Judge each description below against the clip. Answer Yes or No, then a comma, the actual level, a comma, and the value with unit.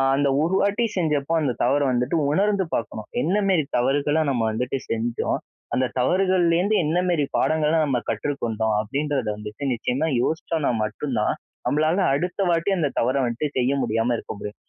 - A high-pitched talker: No, medium, 145 Hz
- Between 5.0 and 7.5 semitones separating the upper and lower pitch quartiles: Yes, wide, 5.6 semitones